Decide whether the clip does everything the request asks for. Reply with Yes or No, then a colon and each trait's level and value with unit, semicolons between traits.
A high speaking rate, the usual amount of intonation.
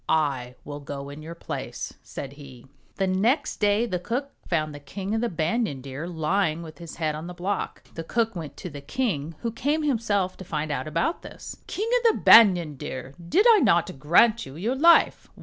No: fast, 210 wpm; wide, 7.1 semitones